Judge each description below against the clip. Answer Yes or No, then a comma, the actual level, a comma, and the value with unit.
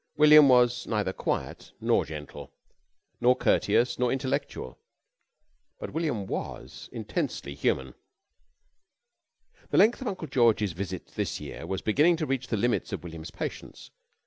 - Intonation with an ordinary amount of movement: No, wide, 7.4 semitones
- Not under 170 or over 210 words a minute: No, slow, 135 wpm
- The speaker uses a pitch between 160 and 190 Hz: No, low, 120 Hz